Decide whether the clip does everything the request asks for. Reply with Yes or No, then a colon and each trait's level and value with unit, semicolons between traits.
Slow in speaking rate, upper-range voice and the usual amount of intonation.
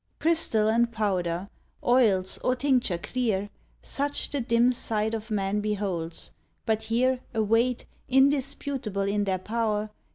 Yes: slow, 125 wpm; high, 220 Hz; average, 3.8 semitones